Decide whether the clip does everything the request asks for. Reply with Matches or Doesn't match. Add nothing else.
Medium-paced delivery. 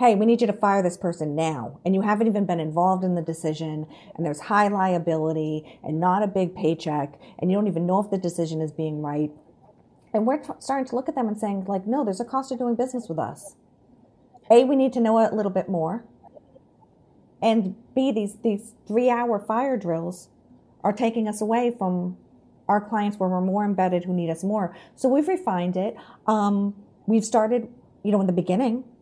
Doesn't match